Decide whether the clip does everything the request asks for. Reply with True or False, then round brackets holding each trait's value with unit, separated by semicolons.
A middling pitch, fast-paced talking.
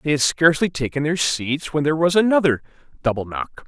False (150 Hz; 195 wpm)